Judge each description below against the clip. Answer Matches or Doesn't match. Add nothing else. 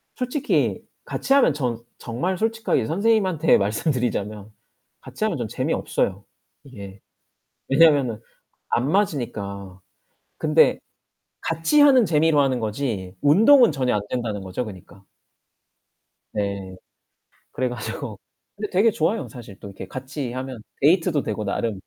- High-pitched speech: Doesn't match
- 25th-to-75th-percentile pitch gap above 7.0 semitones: Matches